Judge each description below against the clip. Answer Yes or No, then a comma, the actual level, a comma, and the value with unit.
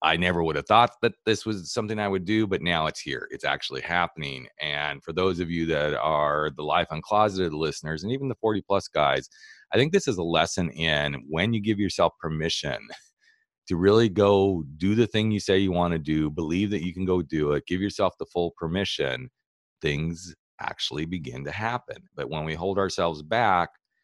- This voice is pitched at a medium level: No, very low, 90 Hz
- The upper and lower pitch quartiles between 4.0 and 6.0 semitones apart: Yes, average, 4.9 semitones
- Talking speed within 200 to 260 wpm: Yes, fast, 205 wpm